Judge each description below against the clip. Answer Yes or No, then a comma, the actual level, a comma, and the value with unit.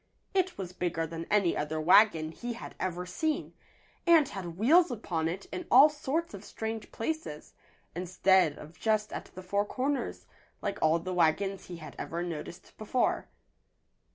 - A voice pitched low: No, high, 190 Hz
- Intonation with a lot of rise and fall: Yes, wide, 6.3 semitones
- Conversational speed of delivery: Yes, average, 160 wpm